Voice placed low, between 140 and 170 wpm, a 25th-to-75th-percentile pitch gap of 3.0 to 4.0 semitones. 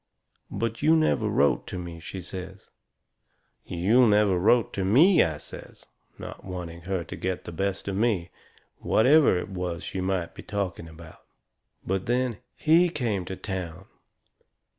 No: very low, 95 Hz; average, 155 wpm; average, 4.4 semitones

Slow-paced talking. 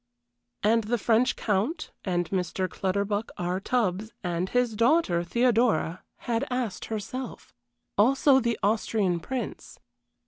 Yes: slow, 115 wpm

